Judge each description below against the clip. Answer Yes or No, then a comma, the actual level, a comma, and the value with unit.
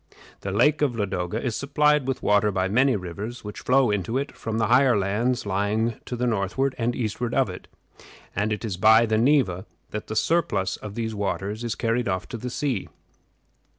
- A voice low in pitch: Yes, low, 110 Hz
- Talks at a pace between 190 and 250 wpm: Yes, average, 195 wpm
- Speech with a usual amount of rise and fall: Yes, average, 3.4 semitones